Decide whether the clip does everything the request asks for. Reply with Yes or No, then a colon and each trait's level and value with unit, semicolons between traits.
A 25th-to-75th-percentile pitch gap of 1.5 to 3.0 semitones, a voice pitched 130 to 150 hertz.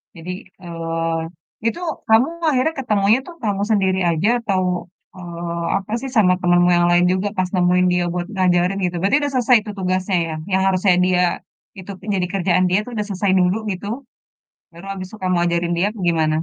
No: narrow, 2.4 semitones; medium, 185 Hz